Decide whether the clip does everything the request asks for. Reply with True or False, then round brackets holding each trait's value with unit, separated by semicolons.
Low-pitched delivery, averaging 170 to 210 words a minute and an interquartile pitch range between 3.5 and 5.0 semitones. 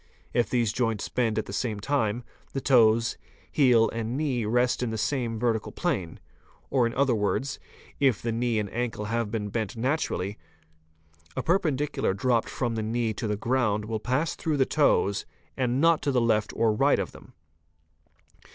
False (115 Hz; 180 wpm; 3.1 semitones)